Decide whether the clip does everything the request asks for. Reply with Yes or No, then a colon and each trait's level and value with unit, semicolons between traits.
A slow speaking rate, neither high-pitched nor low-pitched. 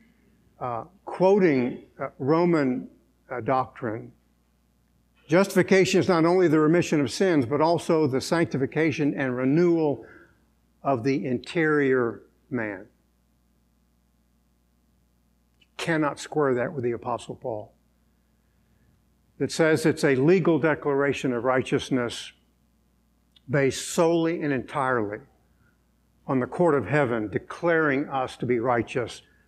No: slow, 105 wpm; low, 130 Hz